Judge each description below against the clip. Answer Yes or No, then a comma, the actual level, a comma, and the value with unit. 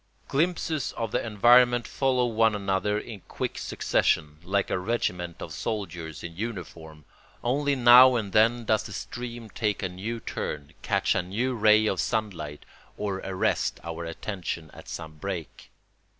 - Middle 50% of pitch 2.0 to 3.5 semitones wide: No, average, 5.1 semitones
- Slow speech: No, average, 150 wpm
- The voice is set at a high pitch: No, low, 105 Hz